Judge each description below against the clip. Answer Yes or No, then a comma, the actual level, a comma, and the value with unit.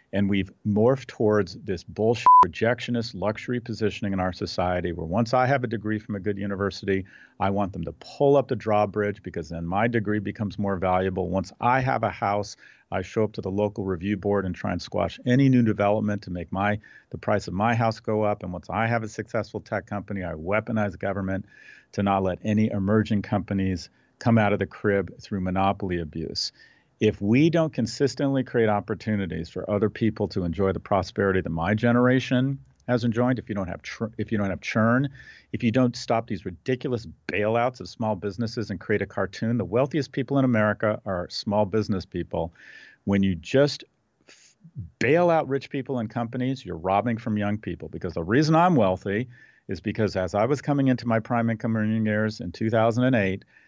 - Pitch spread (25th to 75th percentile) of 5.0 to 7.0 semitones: No, average, 3.4 semitones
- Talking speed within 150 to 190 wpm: No, average, 200 wpm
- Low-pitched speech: Yes, low, 105 Hz